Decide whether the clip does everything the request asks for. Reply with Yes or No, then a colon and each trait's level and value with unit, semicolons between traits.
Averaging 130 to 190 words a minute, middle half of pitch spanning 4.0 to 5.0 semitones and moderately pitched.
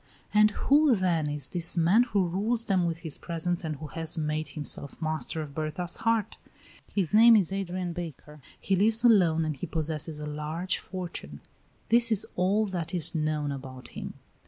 Yes: average, 180 wpm; average, 4.3 semitones; medium, 170 Hz